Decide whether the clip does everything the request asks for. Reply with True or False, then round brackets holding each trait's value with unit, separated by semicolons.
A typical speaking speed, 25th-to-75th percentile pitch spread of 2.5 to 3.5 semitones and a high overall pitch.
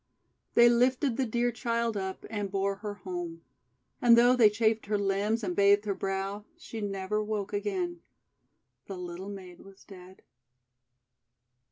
True (150 wpm; 3.1 semitones; 205 Hz)